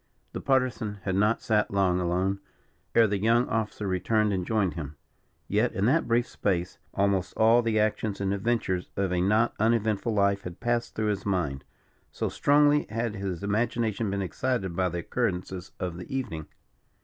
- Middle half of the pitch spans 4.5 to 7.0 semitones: No, average, 3.5 semitones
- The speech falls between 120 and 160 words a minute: No, average, 175 wpm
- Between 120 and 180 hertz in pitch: No, low, 100 Hz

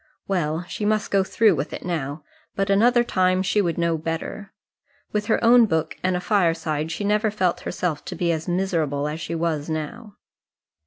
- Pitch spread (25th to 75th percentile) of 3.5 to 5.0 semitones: Yes, average, 4.1 semitones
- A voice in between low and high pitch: Yes, medium, 180 Hz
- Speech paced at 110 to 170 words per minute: No, average, 180 wpm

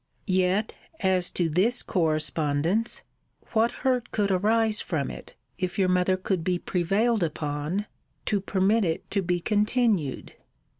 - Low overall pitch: No, high, 190 Hz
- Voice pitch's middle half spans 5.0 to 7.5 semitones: No, average, 4.0 semitones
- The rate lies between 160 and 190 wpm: No, slow, 135 wpm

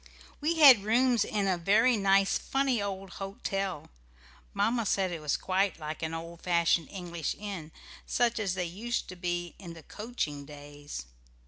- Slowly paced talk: No, average, 160 wpm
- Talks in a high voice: Yes, high, 195 Hz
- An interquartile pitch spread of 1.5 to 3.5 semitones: No, average, 4.4 semitones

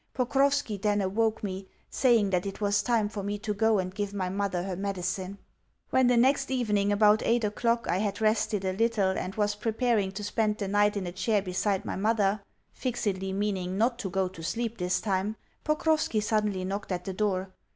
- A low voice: No, high, 205 Hz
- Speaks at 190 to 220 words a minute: Yes, average, 200 wpm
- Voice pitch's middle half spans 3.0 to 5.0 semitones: No, narrow, 2.6 semitones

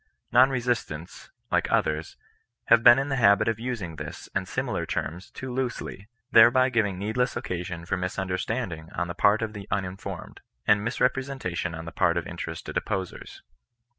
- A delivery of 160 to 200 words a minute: Yes, average, 165 wpm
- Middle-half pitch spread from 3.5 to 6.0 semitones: Yes, wide, 5.5 semitones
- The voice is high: No, low, 100 Hz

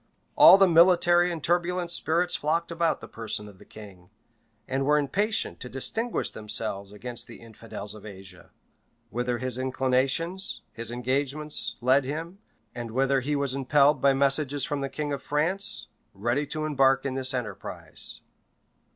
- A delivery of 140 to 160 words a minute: Yes, average, 155 wpm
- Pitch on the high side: No, low, 135 Hz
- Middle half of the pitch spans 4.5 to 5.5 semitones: Yes, average, 4.8 semitones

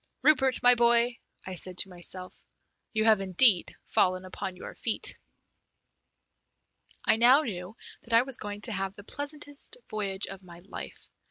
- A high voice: Yes, high, 210 Hz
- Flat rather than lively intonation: No, average, 4.6 semitones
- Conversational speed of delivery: Yes, average, 155 wpm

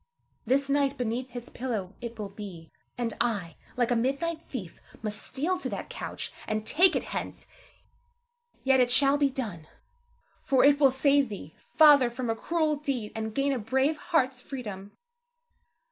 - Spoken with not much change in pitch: No, average, 4.2 semitones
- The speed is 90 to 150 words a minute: No, average, 165 wpm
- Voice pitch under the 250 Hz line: No, very high, 255 Hz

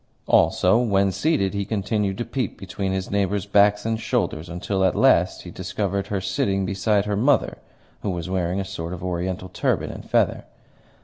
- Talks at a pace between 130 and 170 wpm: No, average, 180 wpm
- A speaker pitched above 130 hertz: No, very low, 95 Hz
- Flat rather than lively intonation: Yes, narrow, 1.8 semitones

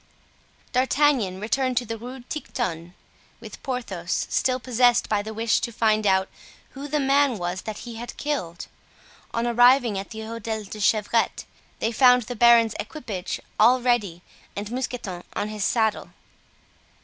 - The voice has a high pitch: Yes, high, 230 Hz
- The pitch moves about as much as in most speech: Yes, average, 3.2 semitones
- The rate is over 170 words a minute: No, average, 155 wpm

